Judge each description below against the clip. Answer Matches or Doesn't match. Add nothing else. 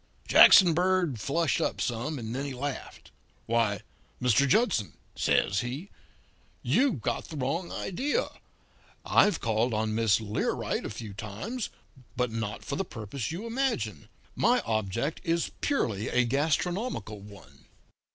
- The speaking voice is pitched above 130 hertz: Doesn't match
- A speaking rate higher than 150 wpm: Doesn't match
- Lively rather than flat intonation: Matches